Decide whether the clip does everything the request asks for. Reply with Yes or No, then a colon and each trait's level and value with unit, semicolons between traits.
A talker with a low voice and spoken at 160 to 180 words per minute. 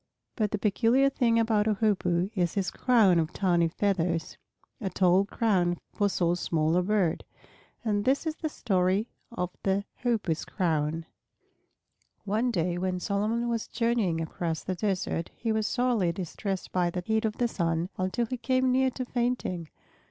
No: high, 200 Hz; average, 165 wpm